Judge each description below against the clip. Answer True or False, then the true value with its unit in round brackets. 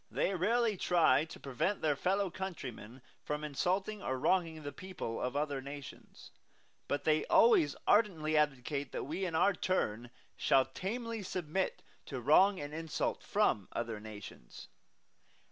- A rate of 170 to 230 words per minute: False (145 wpm)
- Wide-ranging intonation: True (5.7 semitones)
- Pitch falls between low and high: True (155 Hz)